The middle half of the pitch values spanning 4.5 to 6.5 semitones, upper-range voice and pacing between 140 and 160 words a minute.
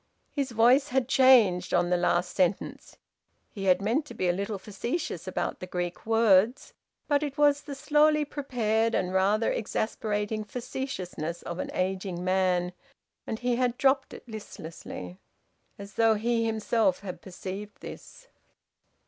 Yes: average, 5.2 semitones; high, 215 Hz; average, 150 wpm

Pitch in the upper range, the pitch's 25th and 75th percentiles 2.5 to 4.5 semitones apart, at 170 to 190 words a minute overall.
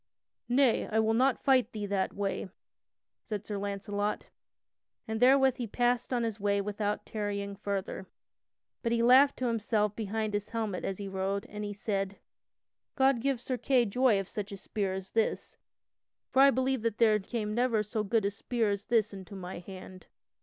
Yes: high, 210 Hz; average, 2.9 semitones; average, 180 wpm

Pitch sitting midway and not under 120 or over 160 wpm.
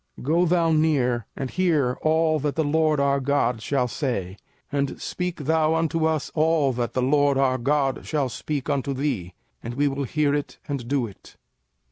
No: medium, 145 Hz; average, 185 wpm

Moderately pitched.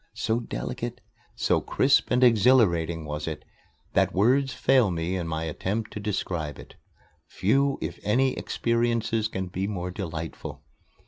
No: low, 105 Hz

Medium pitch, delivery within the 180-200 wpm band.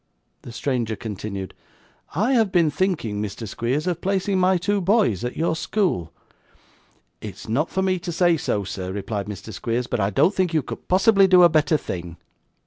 Yes: medium, 155 Hz; average, 190 wpm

